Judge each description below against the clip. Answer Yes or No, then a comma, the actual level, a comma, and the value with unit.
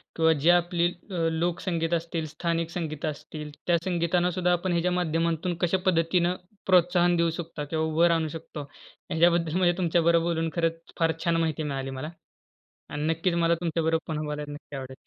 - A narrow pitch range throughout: Yes, narrow, 1.6 semitones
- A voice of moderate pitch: Yes, medium, 165 Hz